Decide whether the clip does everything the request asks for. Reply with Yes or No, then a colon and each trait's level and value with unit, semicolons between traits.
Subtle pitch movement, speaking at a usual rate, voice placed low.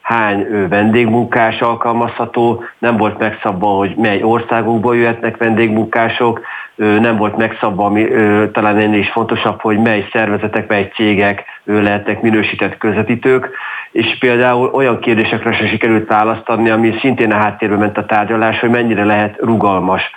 Yes: narrow, 1.8 semitones; average, 135 wpm; low, 110 Hz